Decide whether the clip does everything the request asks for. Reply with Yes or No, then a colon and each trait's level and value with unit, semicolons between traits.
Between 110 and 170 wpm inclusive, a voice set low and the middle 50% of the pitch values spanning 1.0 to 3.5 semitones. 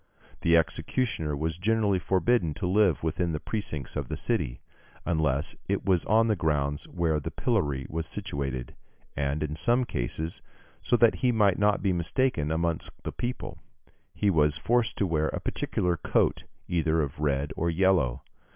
No: average, 165 wpm; very low, 85 Hz; average, 5.2 semitones